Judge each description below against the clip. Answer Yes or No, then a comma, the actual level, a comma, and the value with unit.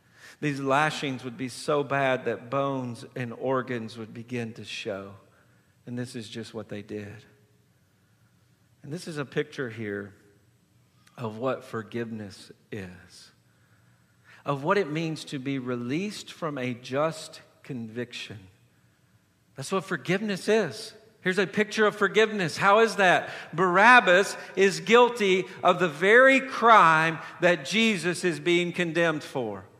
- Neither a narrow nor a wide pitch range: No, wide, 7.6 semitones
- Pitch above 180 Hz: No, medium, 140 Hz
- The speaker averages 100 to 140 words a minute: Yes, slow, 135 wpm